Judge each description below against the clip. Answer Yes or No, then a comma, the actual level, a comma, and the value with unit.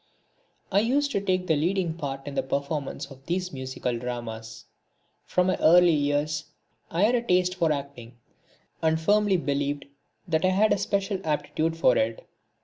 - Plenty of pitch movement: No, average, 4.8 semitones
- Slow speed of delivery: No, average, 165 wpm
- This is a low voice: No, medium, 160 Hz